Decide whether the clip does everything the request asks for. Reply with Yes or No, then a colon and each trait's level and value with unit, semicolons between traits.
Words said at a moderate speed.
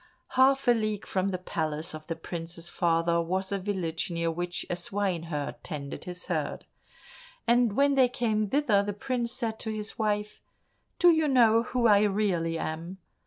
Yes: average, 170 wpm